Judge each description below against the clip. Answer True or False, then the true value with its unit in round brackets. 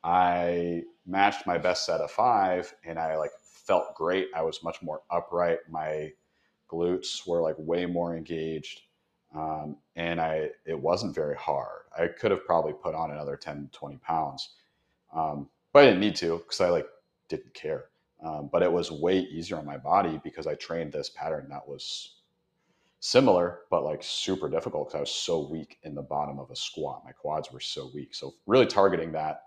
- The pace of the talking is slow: False (190 wpm)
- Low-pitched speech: True (85 Hz)